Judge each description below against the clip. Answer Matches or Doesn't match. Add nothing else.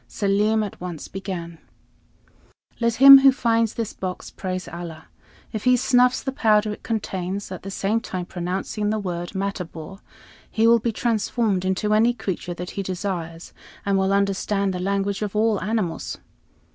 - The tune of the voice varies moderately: Matches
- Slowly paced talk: Doesn't match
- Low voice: Doesn't match